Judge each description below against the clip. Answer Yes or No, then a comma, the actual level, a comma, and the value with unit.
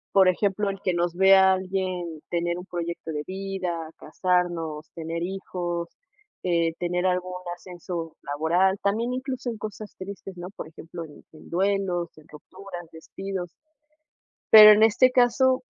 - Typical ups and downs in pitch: No, narrow, 2.3 semitones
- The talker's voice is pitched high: No, medium, 180 Hz